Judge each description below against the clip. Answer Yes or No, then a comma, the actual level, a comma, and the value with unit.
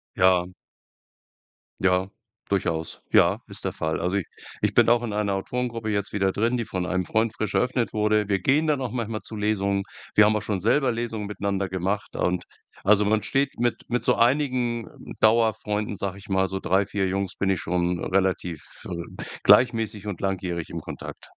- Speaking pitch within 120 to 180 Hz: No, low, 105 Hz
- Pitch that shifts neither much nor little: Yes, average, 3.3 semitones